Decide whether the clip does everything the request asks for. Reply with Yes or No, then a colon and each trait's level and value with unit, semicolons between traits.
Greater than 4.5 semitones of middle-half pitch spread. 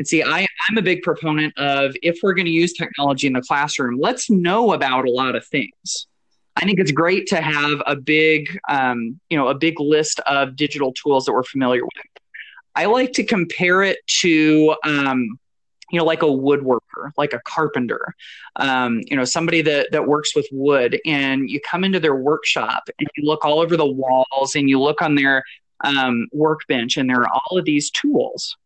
No: average, 3.6 semitones